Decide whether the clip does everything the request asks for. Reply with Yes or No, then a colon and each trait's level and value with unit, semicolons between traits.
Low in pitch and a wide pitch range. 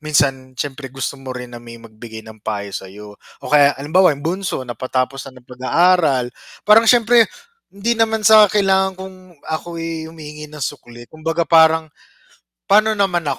No: medium, 155 Hz; wide, 6.4 semitones